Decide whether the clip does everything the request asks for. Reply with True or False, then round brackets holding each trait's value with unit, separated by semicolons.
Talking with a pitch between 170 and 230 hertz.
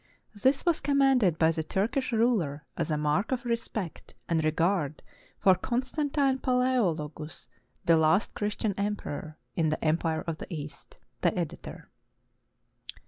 True (190 Hz)